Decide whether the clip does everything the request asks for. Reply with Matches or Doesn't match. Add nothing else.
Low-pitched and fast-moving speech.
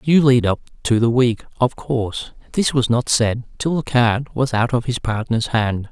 Matches